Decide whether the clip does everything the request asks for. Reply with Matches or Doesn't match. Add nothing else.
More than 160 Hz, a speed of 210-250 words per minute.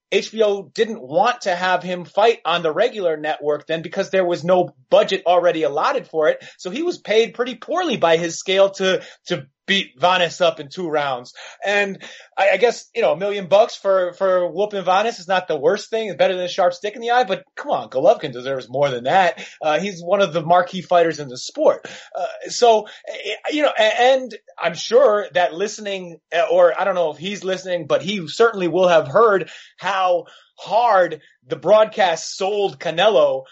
Doesn't match